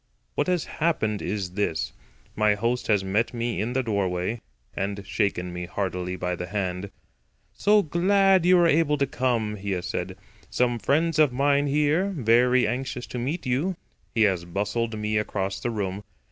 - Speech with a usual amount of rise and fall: No, wide, 6.3 semitones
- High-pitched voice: No, low, 115 Hz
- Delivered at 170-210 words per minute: Yes, average, 175 wpm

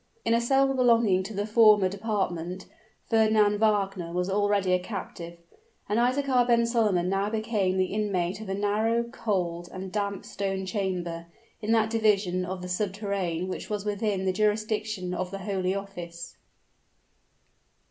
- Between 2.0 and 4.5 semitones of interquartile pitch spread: Yes, average, 2.9 semitones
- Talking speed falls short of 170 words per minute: Yes, average, 150 wpm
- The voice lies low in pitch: No, high, 200 Hz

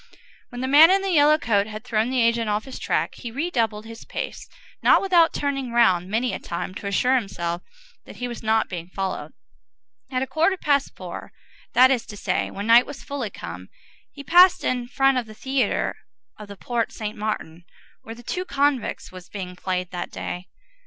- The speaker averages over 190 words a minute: Yes, average, 200 wpm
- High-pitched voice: Yes, high, 235 Hz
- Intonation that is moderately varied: Yes, average, 5.0 semitones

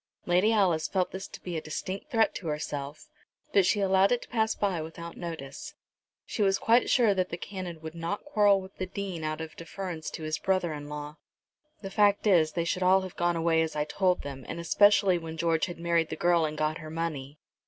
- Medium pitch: Yes, medium, 170 Hz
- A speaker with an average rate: No, fast, 225 wpm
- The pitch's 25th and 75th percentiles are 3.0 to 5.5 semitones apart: Yes, average, 3.4 semitones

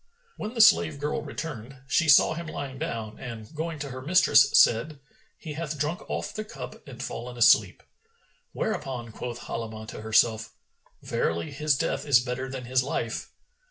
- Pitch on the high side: No, low, 135 Hz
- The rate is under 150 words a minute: No, average, 165 wpm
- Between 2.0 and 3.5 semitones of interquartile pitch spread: No, average, 4.9 semitones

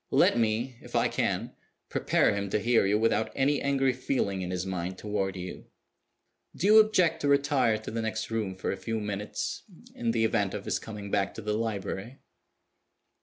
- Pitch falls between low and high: No, low, 110 Hz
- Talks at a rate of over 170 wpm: Yes, average, 190 wpm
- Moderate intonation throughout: Yes, average, 3.9 semitones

